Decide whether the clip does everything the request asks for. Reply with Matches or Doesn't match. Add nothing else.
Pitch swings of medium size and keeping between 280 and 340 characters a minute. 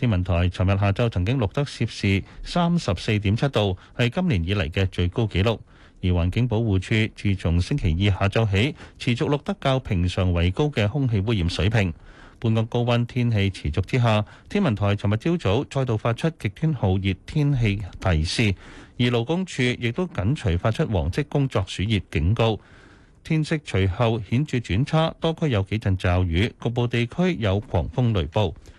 Doesn't match